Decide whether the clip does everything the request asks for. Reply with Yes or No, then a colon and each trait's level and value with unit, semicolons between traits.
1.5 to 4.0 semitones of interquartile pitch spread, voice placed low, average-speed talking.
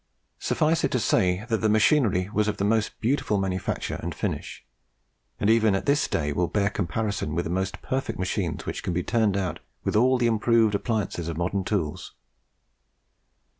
Yes: average, 3.6 semitones; low, 105 Hz; average, 180 wpm